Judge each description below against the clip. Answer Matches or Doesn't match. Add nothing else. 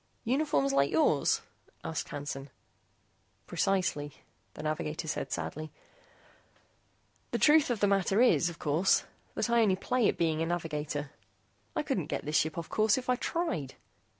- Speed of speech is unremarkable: Matches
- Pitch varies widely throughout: Matches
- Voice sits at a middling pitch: Matches